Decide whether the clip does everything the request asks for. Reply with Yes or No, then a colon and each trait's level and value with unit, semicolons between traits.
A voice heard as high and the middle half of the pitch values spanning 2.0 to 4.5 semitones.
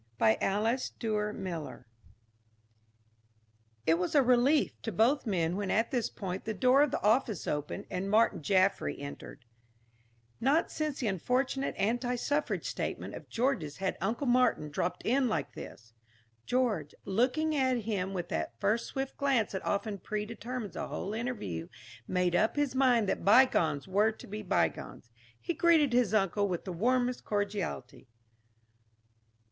No: high, 215 Hz; average, 5.1 semitones